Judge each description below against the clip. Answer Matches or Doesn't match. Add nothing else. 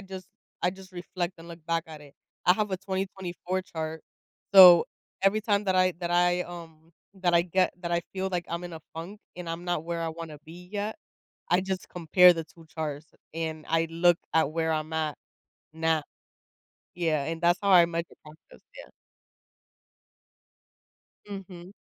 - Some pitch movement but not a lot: Doesn't match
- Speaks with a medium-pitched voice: Matches